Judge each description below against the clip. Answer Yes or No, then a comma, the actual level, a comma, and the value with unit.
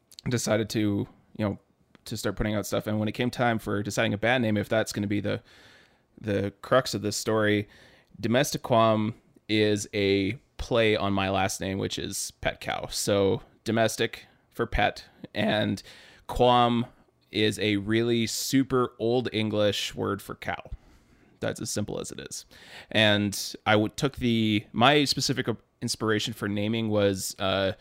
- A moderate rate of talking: Yes, average, 165 wpm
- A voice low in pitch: Yes, low, 110 Hz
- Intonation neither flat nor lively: No, narrow, 2.1 semitones